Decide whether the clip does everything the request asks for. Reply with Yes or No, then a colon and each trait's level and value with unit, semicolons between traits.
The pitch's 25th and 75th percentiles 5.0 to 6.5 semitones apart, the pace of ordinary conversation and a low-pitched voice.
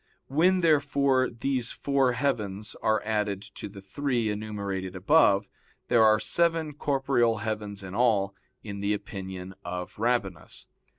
No: average, 5.3 semitones; slow, 130 wpm; low, 110 Hz